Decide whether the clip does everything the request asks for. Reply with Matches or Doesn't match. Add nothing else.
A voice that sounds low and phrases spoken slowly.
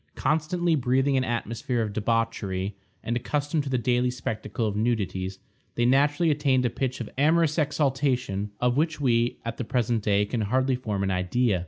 Doesn't match